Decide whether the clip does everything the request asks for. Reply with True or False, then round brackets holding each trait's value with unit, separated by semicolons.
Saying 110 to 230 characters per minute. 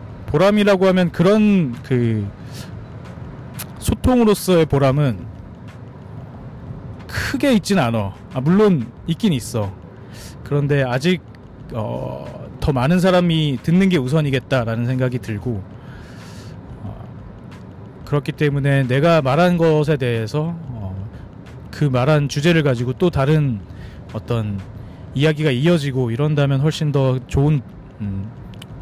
True (225 characters per minute)